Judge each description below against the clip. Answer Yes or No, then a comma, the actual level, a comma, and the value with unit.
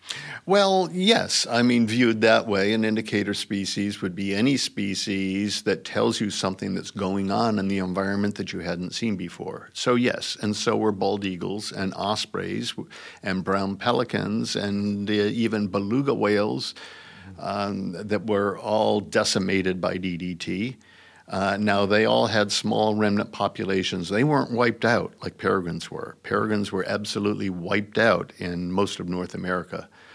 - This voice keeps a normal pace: Yes, average, 155 wpm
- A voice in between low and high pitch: No, low, 100 Hz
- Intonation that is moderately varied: No, narrow, 1.9 semitones